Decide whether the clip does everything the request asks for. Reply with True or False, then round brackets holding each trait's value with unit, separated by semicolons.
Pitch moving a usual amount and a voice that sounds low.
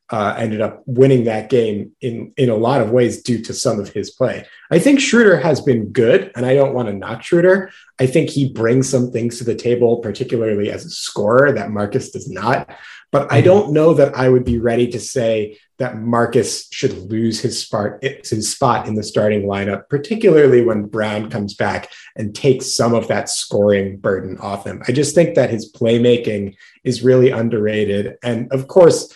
True (3.7 semitones; 120 Hz)